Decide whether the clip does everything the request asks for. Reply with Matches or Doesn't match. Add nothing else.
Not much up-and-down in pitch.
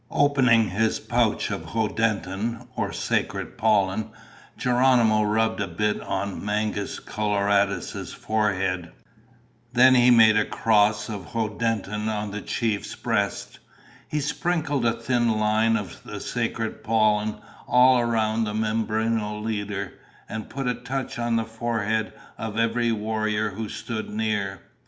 Matches